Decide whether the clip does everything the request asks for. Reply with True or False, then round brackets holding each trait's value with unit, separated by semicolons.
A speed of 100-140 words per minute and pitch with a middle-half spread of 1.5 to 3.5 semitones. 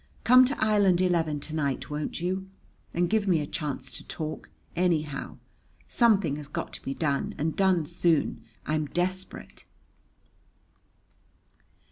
False (135 wpm; 3.9 semitones)